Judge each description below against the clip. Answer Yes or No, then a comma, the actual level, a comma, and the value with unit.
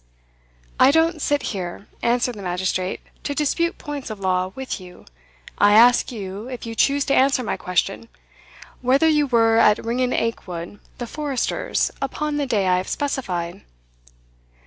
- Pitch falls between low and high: No, high, 235 Hz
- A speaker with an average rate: Yes, average, 155 wpm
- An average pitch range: No, wide, 6.2 semitones